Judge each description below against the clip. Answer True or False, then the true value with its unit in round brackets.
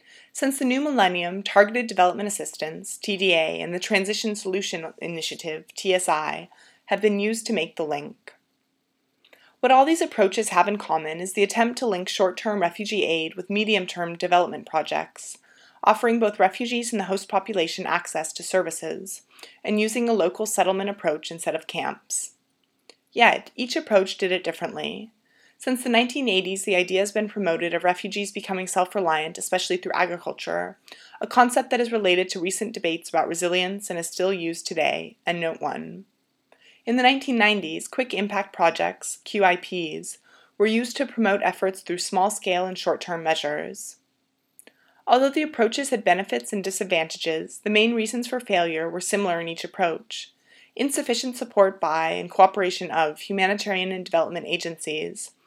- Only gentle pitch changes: False (3.9 semitones)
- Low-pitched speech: False (195 Hz)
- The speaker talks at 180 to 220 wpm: False (155 wpm)